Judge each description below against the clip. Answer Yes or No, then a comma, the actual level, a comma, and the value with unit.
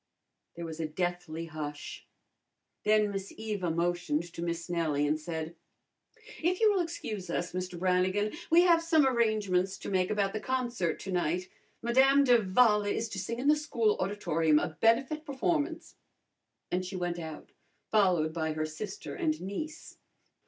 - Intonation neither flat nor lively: No, wide, 5.8 semitones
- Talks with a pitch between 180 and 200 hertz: Yes, high, 190 Hz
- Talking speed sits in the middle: Yes, average, 160 wpm